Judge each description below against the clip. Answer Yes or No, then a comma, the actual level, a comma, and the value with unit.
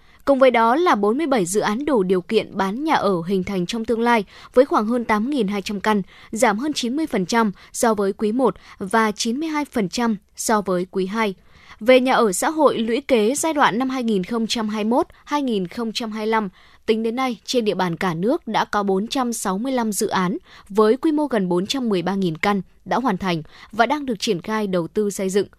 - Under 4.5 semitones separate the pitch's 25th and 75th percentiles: Yes, average, 3.9 semitones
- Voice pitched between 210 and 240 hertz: Yes, high, 220 Hz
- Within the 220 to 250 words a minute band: No, average, 185 wpm